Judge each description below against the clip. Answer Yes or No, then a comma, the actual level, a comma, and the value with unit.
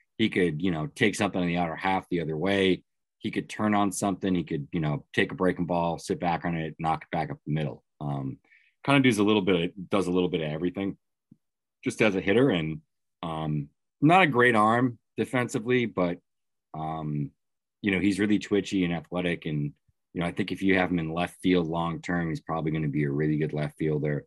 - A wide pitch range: No, average, 4.3 semitones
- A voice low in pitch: Yes, very low, 90 Hz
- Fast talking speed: Yes, fast, 230 wpm